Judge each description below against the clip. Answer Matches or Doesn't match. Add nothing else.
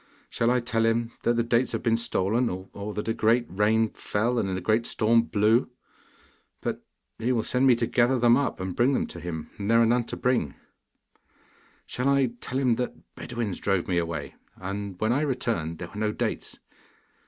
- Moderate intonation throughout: Matches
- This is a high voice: Doesn't match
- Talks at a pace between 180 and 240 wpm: Matches